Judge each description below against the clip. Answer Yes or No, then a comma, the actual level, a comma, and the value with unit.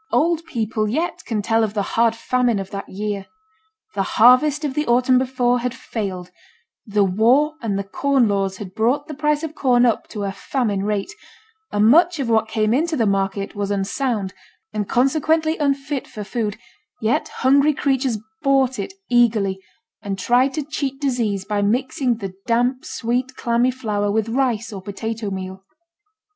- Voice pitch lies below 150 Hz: No, high, 235 Hz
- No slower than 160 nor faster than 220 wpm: Yes, average, 170 wpm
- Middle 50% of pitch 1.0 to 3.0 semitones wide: No, average, 4.6 semitones